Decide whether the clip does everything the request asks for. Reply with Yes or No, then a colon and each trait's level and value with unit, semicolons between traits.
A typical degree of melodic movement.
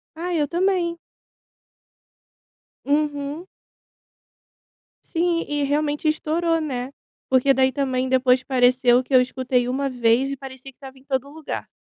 Yes: average, 3.0 semitones